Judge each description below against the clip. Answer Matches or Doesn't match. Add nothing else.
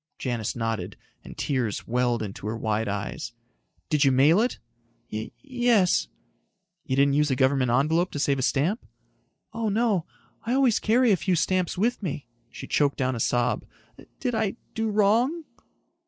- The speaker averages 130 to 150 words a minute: Doesn't match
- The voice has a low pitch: Doesn't match